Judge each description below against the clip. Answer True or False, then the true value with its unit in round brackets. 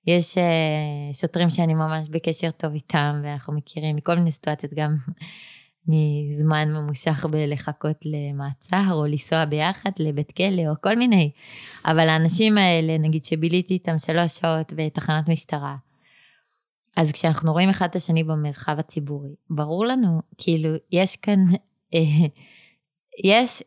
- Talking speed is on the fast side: False (125 wpm)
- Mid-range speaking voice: True (160 Hz)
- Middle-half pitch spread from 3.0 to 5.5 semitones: False (2.4 semitones)